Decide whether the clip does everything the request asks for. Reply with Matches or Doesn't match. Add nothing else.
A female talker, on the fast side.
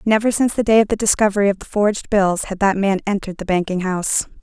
Matches